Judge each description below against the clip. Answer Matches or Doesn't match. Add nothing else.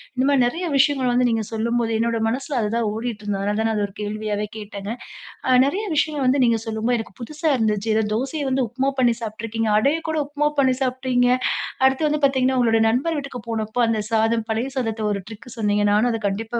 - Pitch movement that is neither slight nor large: Matches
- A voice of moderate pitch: Doesn't match